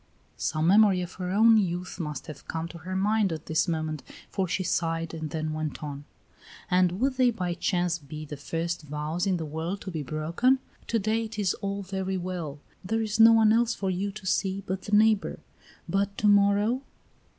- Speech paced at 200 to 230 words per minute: Yes, fast, 205 wpm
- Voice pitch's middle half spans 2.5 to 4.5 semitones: Yes, average, 4.1 semitones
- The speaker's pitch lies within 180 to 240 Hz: Yes, medium, 185 Hz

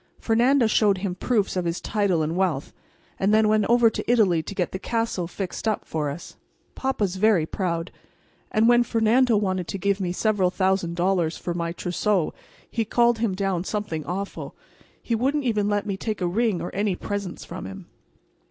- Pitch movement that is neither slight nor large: Yes, average, 3.7 semitones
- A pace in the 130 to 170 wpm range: No, average, 190 wpm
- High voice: Yes, high, 200 Hz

